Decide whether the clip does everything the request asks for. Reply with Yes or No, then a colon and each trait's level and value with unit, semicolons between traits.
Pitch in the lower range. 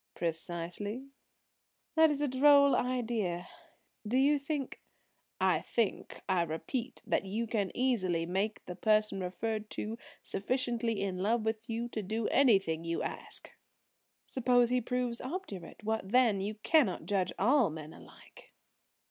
No: high, 220 Hz